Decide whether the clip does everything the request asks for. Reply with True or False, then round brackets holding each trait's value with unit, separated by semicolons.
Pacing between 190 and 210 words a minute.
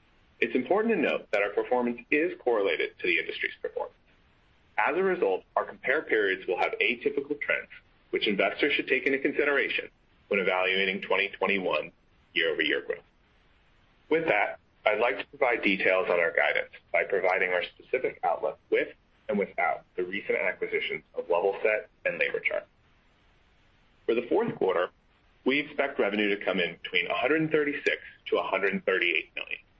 False (155 wpm)